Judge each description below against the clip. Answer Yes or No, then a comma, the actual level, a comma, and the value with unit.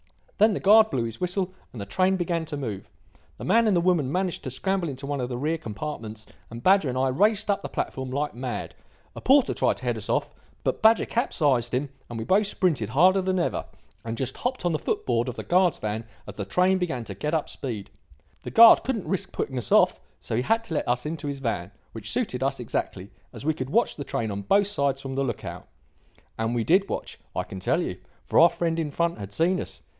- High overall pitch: No, medium, 145 Hz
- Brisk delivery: Yes, fast, 245 wpm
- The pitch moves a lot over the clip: Yes, wide, 7.4 semitones